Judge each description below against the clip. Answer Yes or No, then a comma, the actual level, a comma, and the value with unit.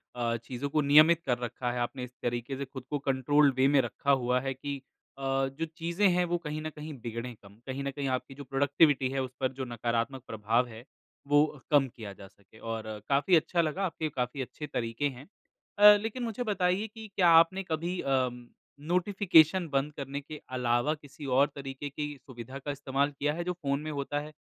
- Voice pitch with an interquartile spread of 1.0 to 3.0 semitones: No, average, 3.7 semitones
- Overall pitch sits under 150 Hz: Yes, medium, 140 Hz